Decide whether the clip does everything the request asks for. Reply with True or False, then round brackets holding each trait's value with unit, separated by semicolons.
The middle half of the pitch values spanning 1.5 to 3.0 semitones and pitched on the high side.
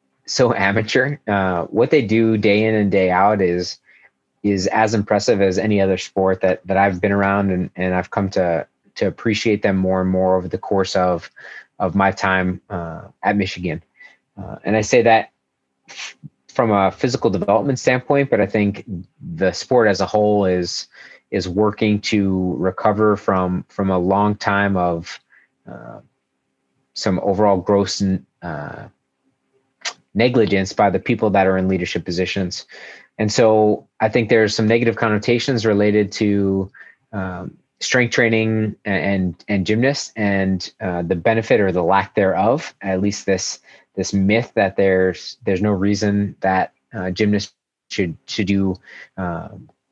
False (2.4 semitones; 100 Hz)